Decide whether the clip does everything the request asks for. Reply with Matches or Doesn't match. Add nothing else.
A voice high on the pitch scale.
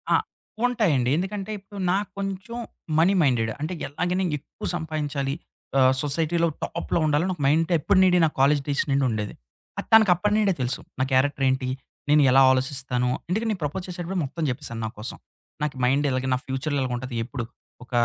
Doesn't match